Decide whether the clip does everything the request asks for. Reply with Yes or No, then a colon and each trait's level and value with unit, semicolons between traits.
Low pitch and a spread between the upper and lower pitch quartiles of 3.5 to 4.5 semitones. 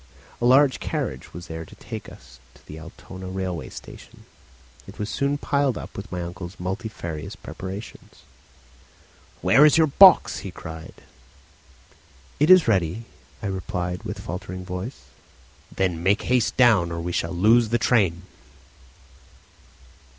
No: very low, 95 Hz; average, 5.3 semitones